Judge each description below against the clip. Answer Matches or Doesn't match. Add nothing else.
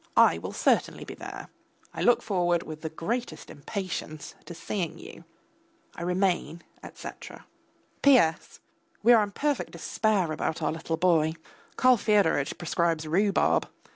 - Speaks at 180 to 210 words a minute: Doesn't match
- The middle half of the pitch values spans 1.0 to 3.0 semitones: Doesn't match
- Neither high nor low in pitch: Matches